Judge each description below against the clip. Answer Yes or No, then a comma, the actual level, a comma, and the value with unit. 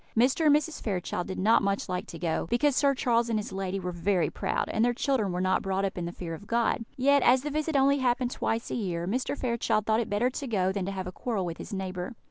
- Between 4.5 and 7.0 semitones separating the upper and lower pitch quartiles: Yes, average, 5.2 semitones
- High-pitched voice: Yes, high, 215 Hz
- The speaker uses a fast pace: Yes, fast, 270 wpm